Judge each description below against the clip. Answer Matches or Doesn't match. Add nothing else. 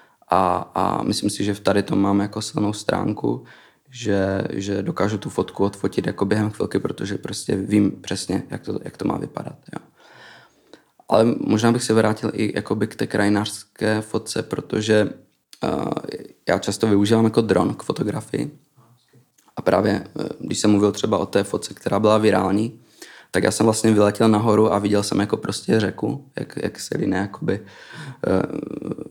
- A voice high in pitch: Doesn't match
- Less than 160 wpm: Doesn't match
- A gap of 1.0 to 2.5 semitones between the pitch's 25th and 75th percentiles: Matches